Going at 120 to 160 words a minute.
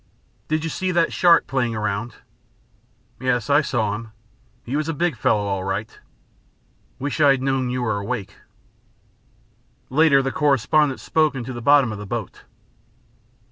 Yes: average, 155 wpm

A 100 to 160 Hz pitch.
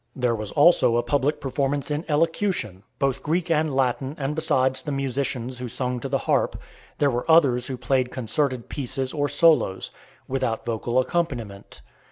Yes: low, 135 Hz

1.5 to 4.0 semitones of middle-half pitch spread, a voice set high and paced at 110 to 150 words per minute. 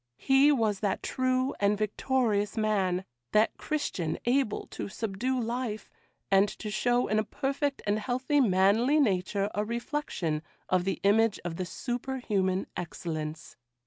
No: average, 4.9 semitones; high, 215 Hz; average, 140 wpm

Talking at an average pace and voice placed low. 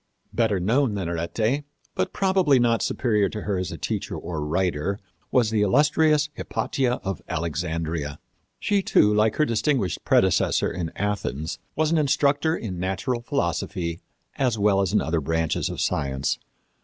Yes: average, 150 wpm; low, 105 Hz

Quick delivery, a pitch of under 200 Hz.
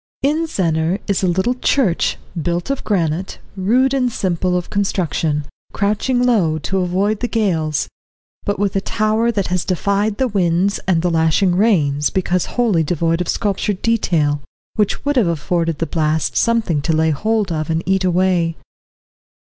No: average, 160 wpm; medium, 185 Hz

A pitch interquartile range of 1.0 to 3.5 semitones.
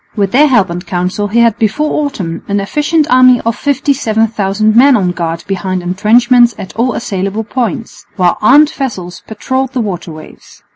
No: average, 5.2 semitones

